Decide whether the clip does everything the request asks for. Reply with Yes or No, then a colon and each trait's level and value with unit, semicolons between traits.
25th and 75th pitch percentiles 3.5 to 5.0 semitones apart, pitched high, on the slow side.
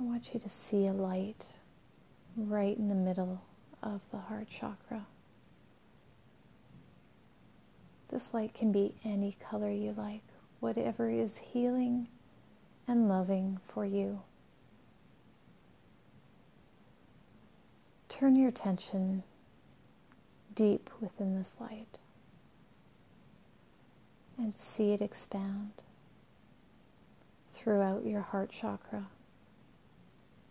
No: average, 2.7 semitones; high, 200 Hz; slow, 90 wpm